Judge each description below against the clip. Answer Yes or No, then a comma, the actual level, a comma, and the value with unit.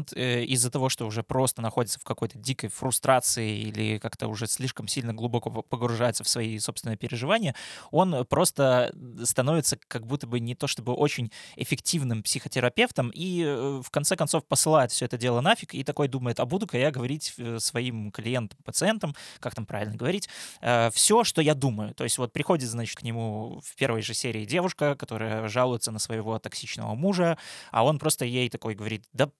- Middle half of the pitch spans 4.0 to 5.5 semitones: Yes, average, 4.3 semitones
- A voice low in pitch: Yes, low, 125 Hz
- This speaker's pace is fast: Yes, fast, 175 wpm